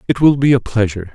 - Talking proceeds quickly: Yes, fast, 260 wpm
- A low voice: Yes, low, 120 Hz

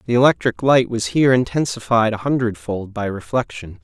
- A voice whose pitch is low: Yes, low, 115 Hz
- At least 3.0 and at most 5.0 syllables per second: No, 5.5 syllables/s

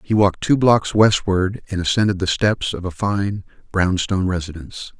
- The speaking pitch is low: Yes, very low, 95 Hz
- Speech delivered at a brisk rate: No, average, 180 wpm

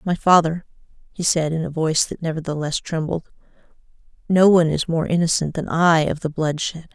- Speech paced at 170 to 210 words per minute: Yes, average, 180 wpm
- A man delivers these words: No, female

